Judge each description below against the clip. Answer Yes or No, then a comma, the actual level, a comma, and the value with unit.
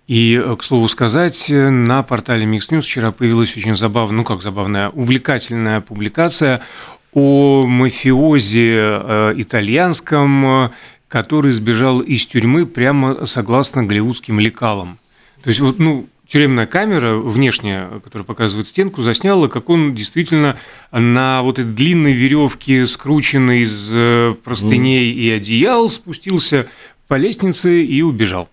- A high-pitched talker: No, low, 125 Hz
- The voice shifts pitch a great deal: No, average, 4.0 semitones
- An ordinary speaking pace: Yes, average, 120 wpm